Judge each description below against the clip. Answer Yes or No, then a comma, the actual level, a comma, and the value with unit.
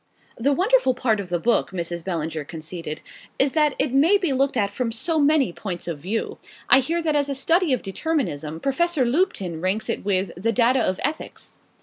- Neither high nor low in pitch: No, high, 240 Hz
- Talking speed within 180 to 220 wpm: Yes, average, 200 wpm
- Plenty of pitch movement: Yes, wide, 8.4 semitones